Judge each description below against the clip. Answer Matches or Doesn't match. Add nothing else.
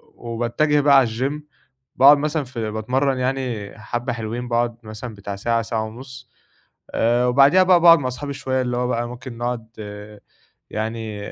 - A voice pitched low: Matches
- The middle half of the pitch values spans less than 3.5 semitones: Matches